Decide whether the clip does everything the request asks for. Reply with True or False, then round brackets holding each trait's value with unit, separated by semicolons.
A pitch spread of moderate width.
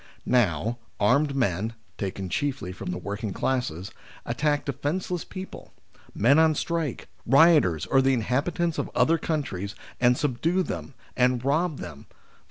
False (7.0 semitones)